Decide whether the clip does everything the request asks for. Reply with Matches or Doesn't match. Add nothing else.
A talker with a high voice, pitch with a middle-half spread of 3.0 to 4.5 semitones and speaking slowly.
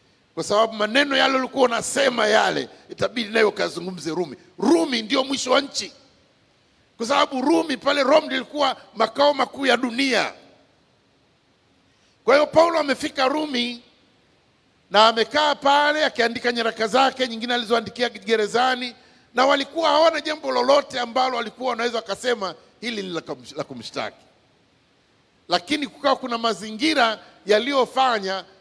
Matches